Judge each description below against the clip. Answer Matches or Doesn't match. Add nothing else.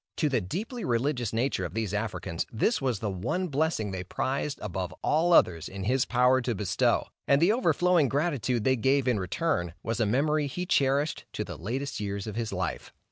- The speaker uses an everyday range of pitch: Doesn't match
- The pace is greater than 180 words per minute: Matches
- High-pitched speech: Doesn't match